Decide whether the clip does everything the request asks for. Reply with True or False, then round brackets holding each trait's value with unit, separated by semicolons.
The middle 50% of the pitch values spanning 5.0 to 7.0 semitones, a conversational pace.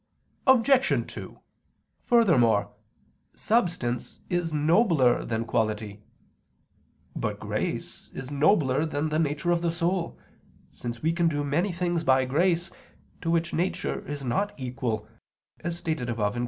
False (5.4 semitones; 130 wpm)